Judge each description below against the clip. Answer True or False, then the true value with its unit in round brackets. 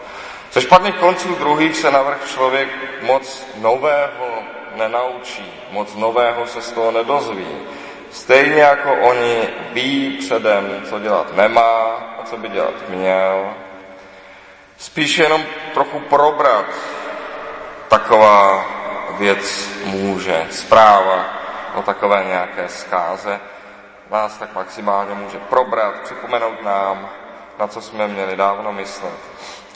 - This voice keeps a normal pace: False (110 wpm)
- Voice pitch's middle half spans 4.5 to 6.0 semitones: True (5.4 semitones)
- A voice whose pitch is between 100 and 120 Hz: True (115 Hz)